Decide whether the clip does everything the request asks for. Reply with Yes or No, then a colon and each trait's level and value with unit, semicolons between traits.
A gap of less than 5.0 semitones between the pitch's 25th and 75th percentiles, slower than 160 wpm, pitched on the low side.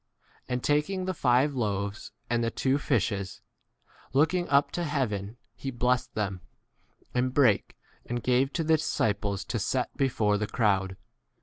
No: average, 5.3 semitones; average, 150 wpm; low, 125 Hz